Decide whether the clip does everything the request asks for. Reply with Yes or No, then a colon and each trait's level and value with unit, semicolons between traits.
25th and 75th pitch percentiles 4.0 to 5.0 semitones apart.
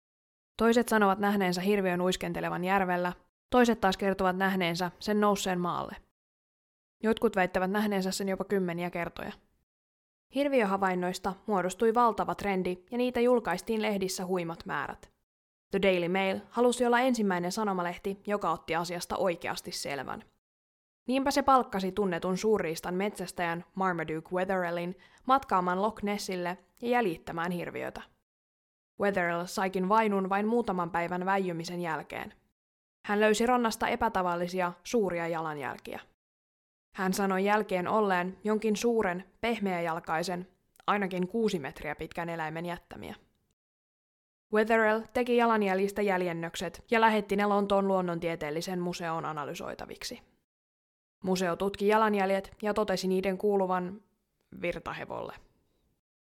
No: average, 3.1 semitones